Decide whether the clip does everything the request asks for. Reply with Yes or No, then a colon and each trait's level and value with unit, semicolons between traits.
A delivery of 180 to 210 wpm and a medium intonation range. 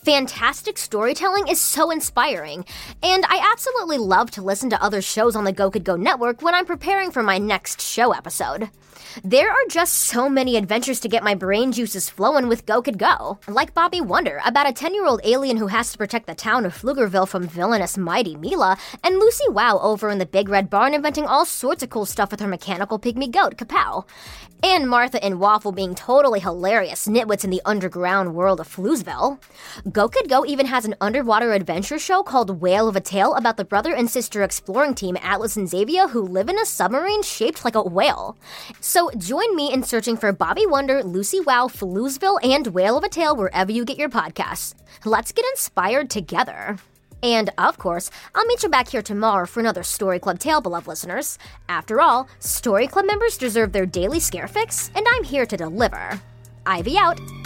No: average, 200 wpm; wide, 6.7 semitones